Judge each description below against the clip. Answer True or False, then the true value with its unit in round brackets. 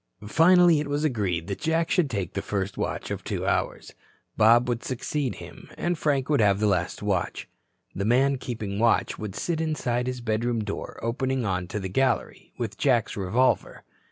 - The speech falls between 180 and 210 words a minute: True (185 wpm)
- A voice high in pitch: False (120 Hz)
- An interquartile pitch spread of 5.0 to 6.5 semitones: True (5.3 semitones)